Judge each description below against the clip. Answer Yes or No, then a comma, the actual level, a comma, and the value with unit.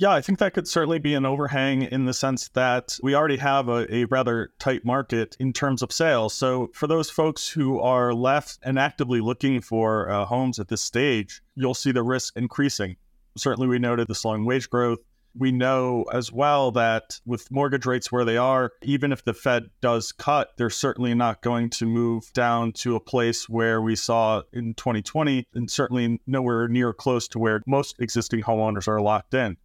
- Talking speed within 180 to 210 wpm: Yes, average, 200 wpm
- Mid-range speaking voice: No, low, 125 Hz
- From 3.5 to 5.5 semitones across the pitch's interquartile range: No, narrow, 2.6 semitones